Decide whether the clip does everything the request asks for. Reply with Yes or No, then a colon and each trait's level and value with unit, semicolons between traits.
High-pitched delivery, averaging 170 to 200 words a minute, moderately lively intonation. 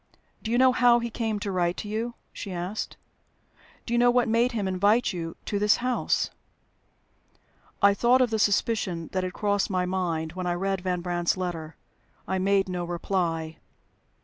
Yes: high, 195 Hz; average, 180 wpm; average, 4.2 semitones